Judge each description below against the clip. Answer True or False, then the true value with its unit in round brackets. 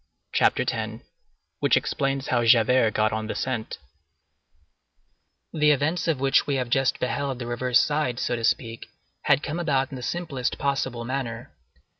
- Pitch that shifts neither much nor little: True (3.0 semitones)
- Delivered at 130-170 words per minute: True (155 wpm)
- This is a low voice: True (130 Hz)